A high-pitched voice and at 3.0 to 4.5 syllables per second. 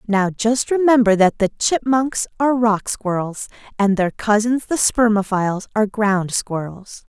Yes: high, 215 Hz; 4.4 syllables/s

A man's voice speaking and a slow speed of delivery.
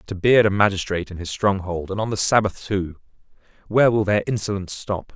No: male; average, 200 wpm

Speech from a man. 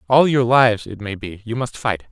Yes: male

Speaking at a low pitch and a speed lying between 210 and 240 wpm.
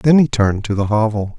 No: low, 115 Hz; fast, 260 wpm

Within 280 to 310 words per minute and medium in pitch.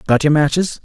No: fast, 215 wpm; medium, 150 Hz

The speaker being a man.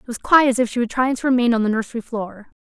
No: female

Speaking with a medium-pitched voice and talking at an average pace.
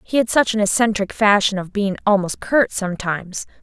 No: high, 205 Hz; average, 180 wpm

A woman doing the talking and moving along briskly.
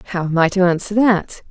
Yes: female; fast, 240 wpm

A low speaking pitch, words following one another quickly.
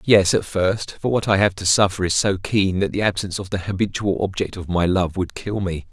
Yes: very low, 95 Hz; fast, 255 wpm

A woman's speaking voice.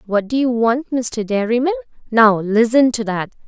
Yes: female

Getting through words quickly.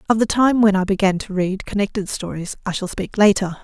Yes: fast, 230 wpm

